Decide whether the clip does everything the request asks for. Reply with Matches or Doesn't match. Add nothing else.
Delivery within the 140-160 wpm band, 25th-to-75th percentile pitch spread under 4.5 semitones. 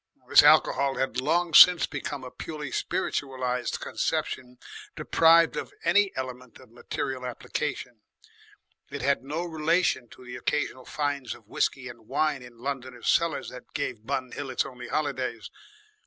Matches